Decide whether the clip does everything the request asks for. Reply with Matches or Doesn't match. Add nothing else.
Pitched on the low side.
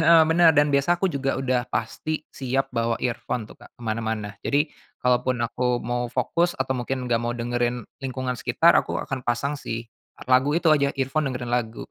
Matches